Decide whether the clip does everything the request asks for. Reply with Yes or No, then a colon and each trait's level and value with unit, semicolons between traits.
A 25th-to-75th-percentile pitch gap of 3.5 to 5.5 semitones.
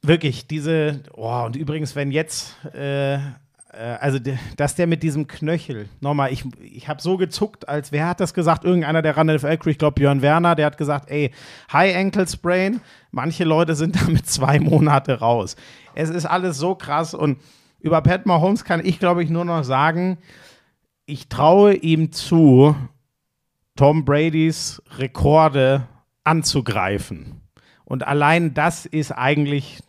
No: average, 3.1 semitones